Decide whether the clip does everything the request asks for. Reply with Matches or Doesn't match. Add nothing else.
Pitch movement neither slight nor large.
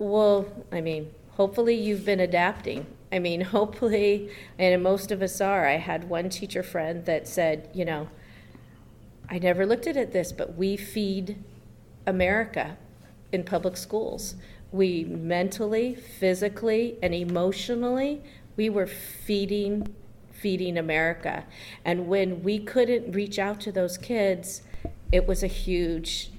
Matches